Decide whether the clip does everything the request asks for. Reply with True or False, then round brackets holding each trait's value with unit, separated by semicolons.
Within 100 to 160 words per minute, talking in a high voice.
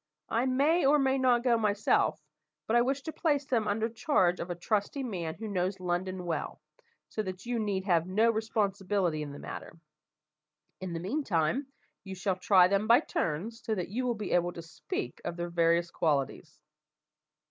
False (185 wpm; 200 Hz)